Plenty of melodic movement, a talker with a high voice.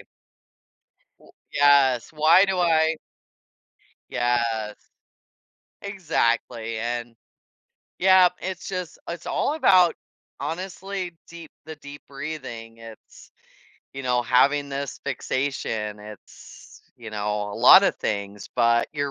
No: wide, 6.5 semitones; medium, 140 Hz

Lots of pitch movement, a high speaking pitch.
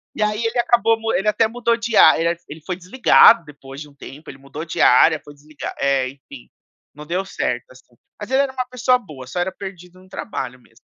No: wide, 7.7 semitones; medium, 180 Hz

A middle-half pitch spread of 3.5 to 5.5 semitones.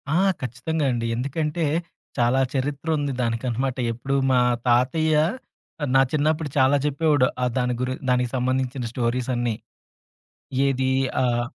No: average, 2.8 semitones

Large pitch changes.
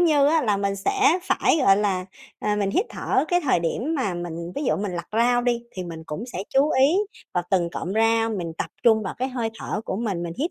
Yes: wide, 6.3 semitones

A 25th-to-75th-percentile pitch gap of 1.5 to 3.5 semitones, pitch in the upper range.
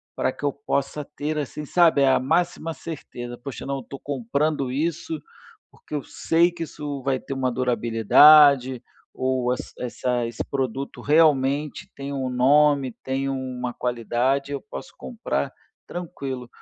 No: average, 2.8 semitones; medium, 140 Hz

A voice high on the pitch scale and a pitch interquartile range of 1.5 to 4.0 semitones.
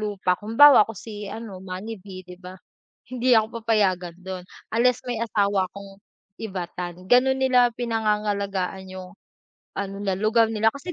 Yes: high, 205 Hz; average, 3.3 semitones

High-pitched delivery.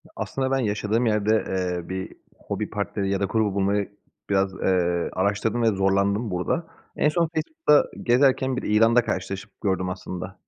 No: low, 100 Hz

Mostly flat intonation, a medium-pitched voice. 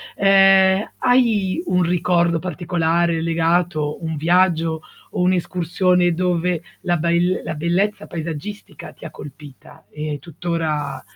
Yes: narrow, 2.1 semitones; medium, 175 Hz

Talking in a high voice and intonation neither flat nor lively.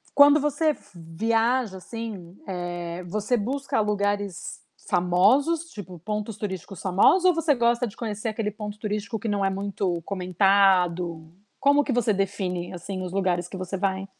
Yes: high, 200 Hz; average, 3.9 semitones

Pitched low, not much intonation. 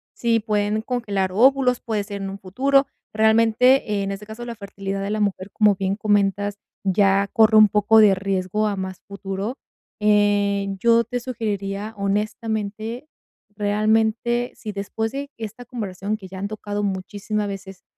No: high, 210 Hz; narrow, 2.0 semitones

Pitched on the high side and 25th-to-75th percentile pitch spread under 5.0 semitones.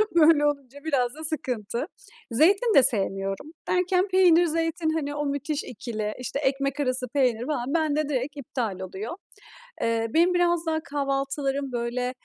Yes: very high, 280 Hz; average, 4.3 semitones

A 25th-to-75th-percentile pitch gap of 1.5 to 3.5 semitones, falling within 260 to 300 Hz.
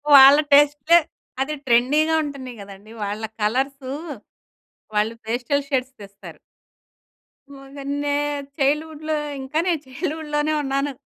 Yes: average, 2.9 semitones; very high, 275 Hz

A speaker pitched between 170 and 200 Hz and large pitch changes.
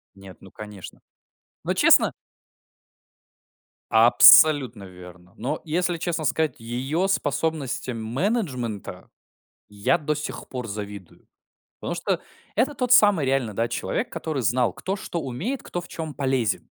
No: low, 130 Hz; wide, 6.7 semitones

